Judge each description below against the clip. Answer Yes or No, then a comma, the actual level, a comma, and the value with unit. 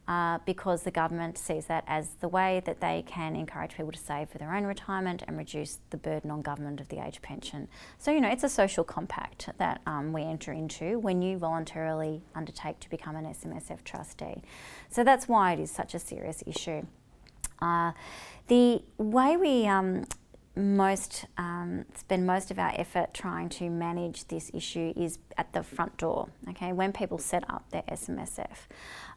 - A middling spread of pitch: Yes, average, 3.6 semitones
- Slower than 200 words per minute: Yes, average, 185 wpm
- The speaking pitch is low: No, medium, 170 Hz